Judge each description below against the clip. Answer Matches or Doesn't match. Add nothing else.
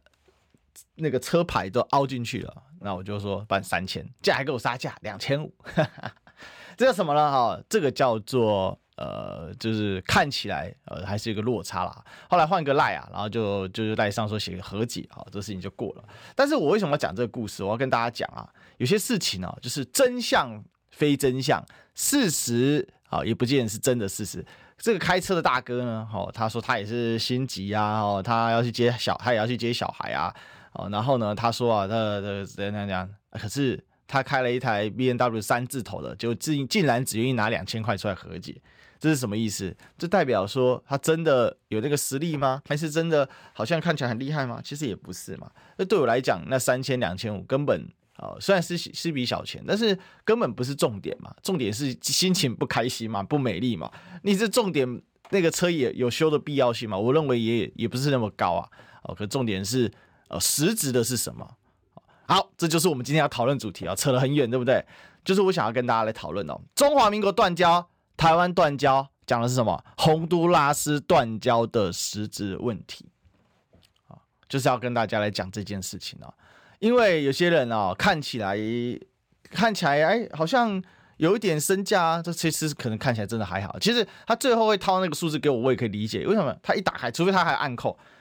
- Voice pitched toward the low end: Matches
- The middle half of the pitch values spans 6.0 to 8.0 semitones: Matches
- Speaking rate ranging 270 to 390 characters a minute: Matches